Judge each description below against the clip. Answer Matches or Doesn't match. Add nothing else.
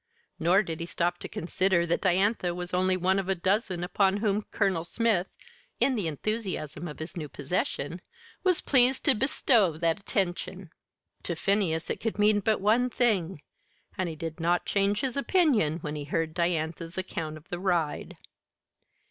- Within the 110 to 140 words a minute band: Doesn't match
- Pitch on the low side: Doesn't match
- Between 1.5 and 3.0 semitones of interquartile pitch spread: Doesn't match